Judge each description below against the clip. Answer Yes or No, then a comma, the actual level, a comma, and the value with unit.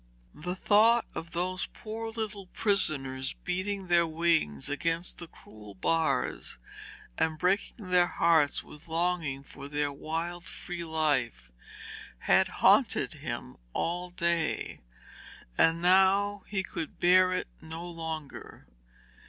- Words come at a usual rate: No, slow, 120 wpm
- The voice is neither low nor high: Yes, medium, 170 Hz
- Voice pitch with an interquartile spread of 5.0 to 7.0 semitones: No, average, 2.8 semitones